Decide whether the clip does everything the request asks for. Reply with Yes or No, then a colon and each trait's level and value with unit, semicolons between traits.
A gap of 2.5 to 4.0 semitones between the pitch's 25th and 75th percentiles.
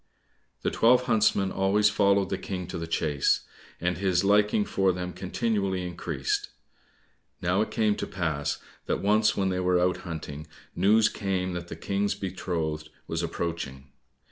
Yes: average, 2.9 semitones